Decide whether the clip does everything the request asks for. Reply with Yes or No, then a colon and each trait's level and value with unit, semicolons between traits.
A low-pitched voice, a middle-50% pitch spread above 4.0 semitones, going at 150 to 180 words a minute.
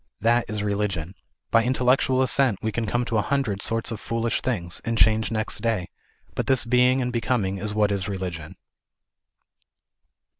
No: low, 110 Hz; average, 3.3 semitones; average, 165 wpm